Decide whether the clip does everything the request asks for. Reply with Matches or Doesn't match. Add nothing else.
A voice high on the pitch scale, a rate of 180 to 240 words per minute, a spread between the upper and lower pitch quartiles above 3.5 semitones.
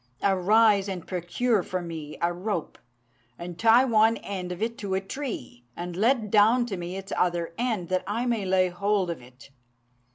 Matches